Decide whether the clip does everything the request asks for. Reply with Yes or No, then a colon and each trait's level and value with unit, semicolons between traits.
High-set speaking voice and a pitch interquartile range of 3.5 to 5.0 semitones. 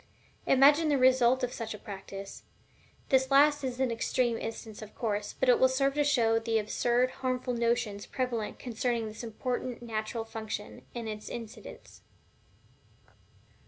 No: high, 235 Hz; average, 2.7 semitones